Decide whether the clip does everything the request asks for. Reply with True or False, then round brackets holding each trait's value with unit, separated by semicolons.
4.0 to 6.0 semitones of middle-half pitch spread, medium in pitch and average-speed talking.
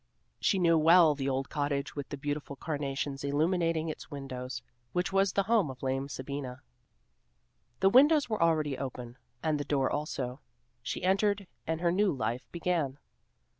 True (4.4 semitones; 150 Hz; 160 wpm)